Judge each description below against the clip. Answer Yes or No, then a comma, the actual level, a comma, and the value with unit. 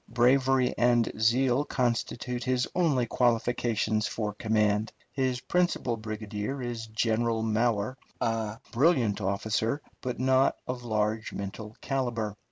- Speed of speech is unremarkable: No, slow, 115 wpm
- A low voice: Yes, low, 115 Hz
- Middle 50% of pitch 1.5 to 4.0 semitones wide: Yes, average, 2.7 semitones